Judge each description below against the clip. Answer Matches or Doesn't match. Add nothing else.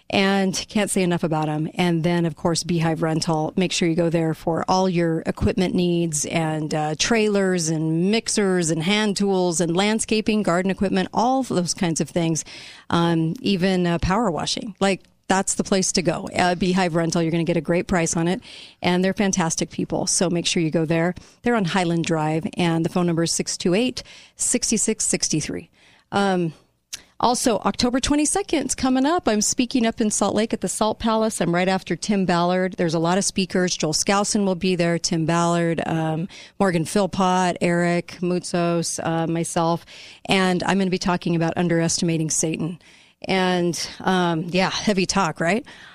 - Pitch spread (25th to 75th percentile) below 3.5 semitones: Matches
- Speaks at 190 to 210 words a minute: Doesn't match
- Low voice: Doesn't match